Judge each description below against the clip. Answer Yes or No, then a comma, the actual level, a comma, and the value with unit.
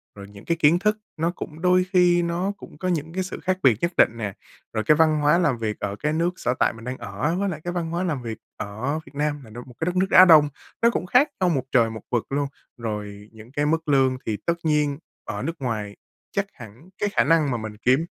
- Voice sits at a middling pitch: Yes, medium, 150 Hz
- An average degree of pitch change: No, wide, 6.8 semitones